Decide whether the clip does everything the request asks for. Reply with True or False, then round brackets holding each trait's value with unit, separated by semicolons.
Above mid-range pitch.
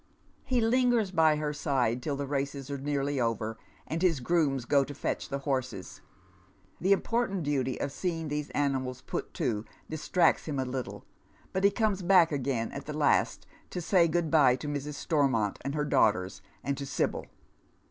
False (145 Hz)